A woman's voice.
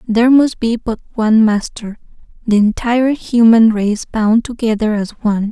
Yes: female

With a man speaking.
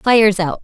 No: female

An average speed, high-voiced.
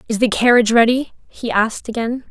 Yes: average, 180 wpm; high, 230 Hz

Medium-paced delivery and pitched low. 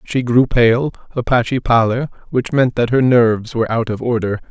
Yes: average, 185 wpm; low, 120 Hz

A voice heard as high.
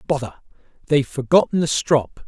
No: medium, 140 Hz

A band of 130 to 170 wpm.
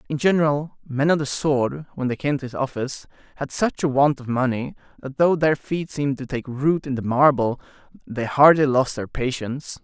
No: fast, 205 wpm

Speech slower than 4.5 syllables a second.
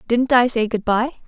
No: 5.3 syllables/s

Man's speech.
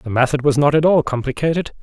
Yes: male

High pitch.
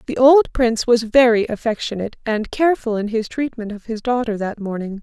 Yes: high, 240 Hz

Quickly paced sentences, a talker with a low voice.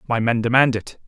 Yes: fast, 225 wpm; low, 120 Hz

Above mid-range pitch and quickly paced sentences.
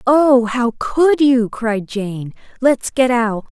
No: high, 240 Hz; average, 150 wpm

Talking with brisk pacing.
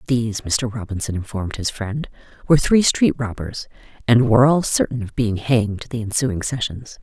No: average, 170 wpm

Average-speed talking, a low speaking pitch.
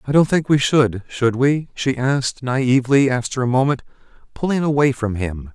Yes: average, 185 wpm; low, 130 Hz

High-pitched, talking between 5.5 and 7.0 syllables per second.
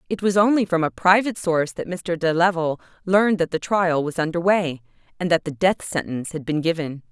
No: medium, 175 Hz; 5.8 syllables/s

